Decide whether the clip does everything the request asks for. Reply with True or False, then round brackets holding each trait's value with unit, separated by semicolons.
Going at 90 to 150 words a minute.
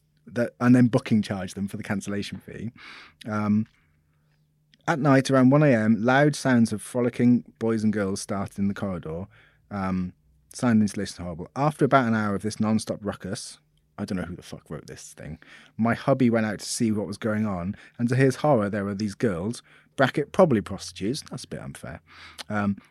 False (200 wpm)